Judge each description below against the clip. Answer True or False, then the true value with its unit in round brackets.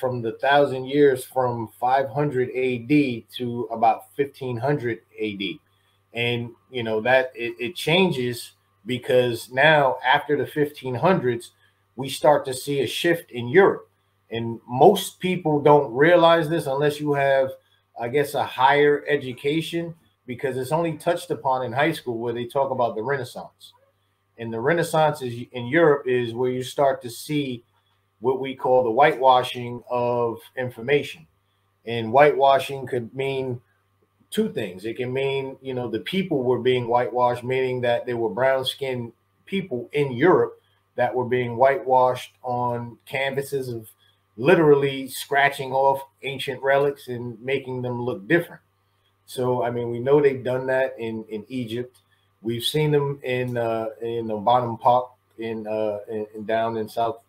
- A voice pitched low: True (125 Hz)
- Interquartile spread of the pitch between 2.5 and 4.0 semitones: True (3.2 semitones)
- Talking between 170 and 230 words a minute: False (150 wpm)